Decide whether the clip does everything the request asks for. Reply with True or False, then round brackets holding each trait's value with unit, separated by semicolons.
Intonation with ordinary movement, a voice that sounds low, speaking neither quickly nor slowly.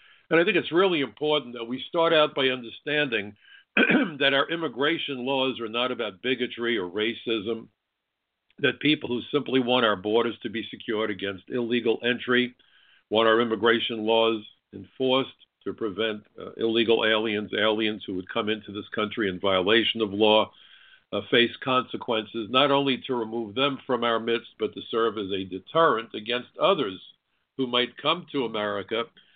True (3.3 semitones; 120 Hz; 165 wpm)